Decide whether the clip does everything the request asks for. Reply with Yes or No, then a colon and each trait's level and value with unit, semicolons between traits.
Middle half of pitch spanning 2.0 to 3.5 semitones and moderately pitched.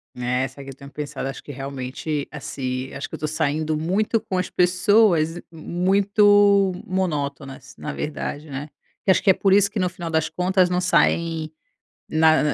No: average, 4.9 semitones; medium, 160 Hz